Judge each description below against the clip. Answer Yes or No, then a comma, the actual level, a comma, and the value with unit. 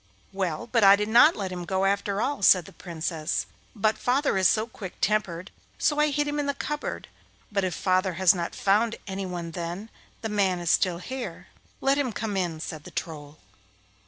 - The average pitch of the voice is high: Yes, high, 195 Hz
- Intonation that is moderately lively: Yes, average, 4.2 semitones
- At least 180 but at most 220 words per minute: Yes, average, 195 wpm